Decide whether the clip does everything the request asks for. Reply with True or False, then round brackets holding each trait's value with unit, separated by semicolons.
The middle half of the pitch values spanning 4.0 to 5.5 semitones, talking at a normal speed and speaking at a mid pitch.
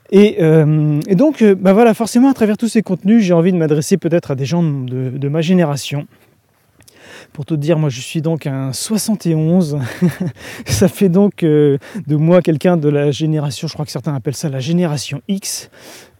True (4.6 semitones; 195 wpm; 165 Hz)